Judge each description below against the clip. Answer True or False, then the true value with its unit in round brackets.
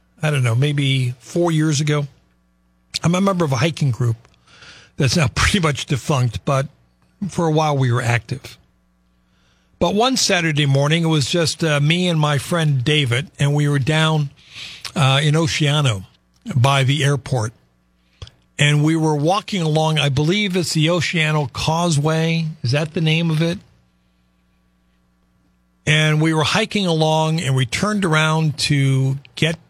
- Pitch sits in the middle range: True (145 Hz)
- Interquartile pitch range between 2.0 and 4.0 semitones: False (5.1 semitones)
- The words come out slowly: False (155 wpm)